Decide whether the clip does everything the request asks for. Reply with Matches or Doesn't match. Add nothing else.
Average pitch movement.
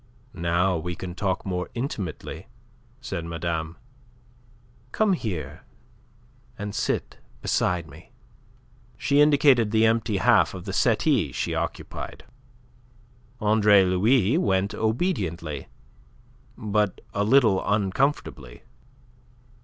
Matches